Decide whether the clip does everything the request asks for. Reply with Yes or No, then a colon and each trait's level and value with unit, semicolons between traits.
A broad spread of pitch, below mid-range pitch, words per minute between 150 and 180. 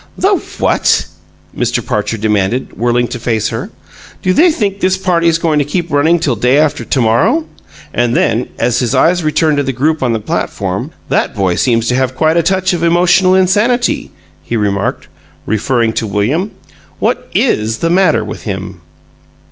No: wide, 7.2 semitones; medium, 145 Hz; average, 175 wpm